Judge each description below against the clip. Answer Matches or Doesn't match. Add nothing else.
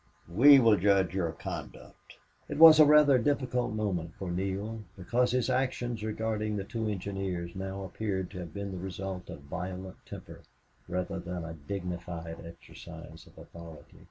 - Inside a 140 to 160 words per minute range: Matches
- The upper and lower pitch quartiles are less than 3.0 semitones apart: Doesn't match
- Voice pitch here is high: Doesn't match